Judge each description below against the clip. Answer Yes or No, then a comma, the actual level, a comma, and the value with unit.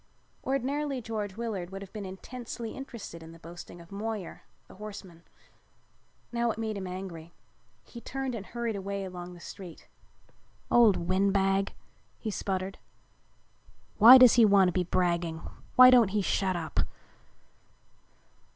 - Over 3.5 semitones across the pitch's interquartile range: Yes, average, 4.1 semitones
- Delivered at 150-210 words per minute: No, average, 140 wpm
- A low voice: No, high, 200 Hz